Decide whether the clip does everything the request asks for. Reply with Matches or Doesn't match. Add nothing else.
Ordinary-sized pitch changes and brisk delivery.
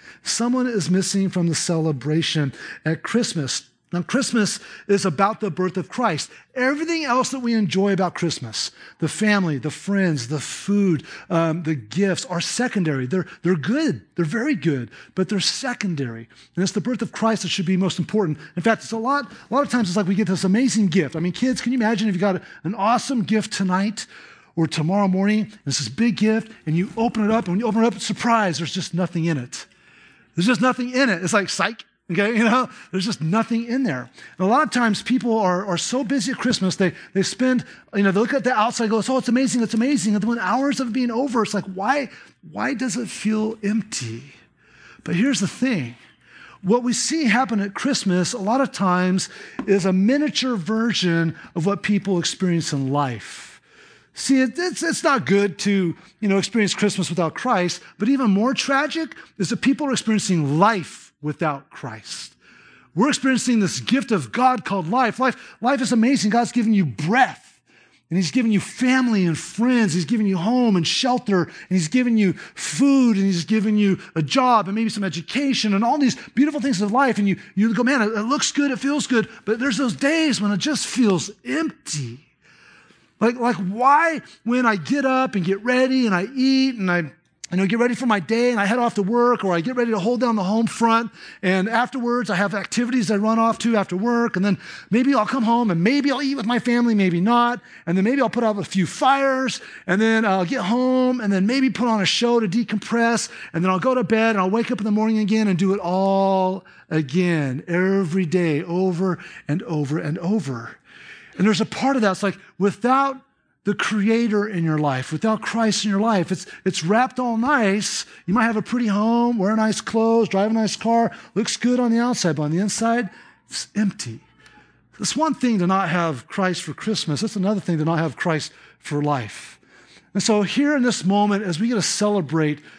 Matches